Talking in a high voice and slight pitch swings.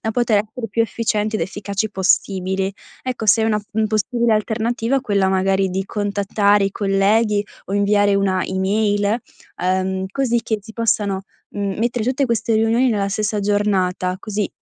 Yes: high, 205 Hz; narrow, 2.3 semitones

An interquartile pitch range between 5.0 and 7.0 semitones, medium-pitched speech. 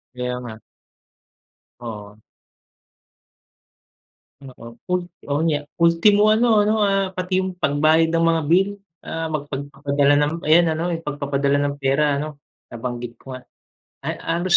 No: average, 4.0 semitones; medium, 150 Hz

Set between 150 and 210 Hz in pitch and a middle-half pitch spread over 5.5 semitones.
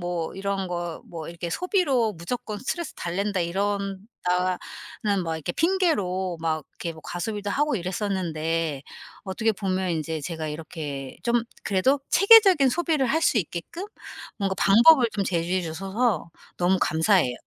No: high, 190 Hz; average, 5.1 semitones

